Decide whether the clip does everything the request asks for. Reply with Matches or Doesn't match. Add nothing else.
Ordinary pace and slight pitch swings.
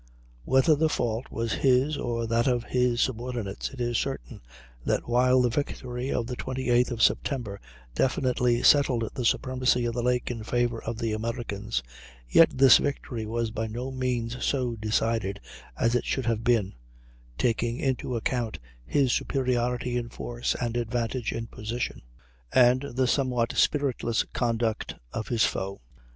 Matches